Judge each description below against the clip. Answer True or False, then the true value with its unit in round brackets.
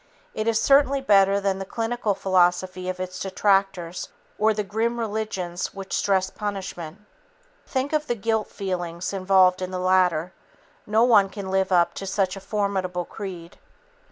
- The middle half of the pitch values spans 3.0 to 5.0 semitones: False (2.6 semitones)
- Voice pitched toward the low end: False (195 Hz)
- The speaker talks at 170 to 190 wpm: False (155 wpm)